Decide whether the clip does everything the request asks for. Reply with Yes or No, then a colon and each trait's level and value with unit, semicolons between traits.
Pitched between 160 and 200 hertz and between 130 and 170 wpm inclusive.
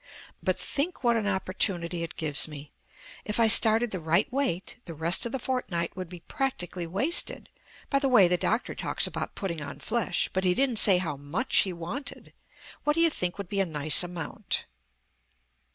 No: medium, 185 Hz; average, 190 wpm